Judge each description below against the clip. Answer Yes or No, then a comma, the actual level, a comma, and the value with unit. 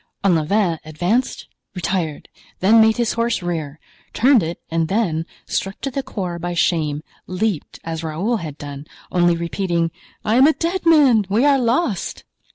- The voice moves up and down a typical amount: No, wide, 5.9 semitones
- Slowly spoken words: No, average, 155 wpm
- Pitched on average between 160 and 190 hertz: Yes, medium, 185 Hz